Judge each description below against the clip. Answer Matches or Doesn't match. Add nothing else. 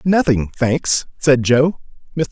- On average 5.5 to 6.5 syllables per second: Doesn't match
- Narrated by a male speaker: Matches